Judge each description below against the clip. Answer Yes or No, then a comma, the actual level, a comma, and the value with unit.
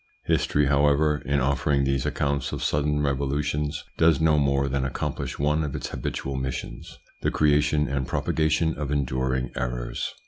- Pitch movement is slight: Yes, narrow, 1.7 semitones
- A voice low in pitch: Yes, very low, 70 Hz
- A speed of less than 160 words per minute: Yes, average, 150 wpm